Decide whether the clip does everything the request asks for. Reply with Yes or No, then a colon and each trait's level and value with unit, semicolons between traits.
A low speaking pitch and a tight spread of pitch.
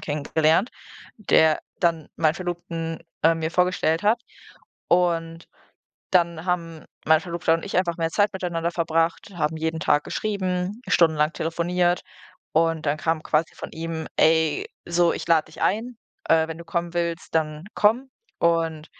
No: medium, 165 Hz; narrow, 1.7 semitones